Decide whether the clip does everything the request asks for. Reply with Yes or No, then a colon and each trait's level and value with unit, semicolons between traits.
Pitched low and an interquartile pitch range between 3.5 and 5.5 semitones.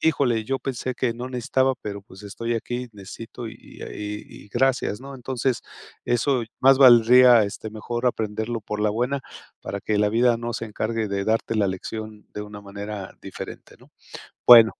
No: low, 115 Hz; average, 2.9 semitones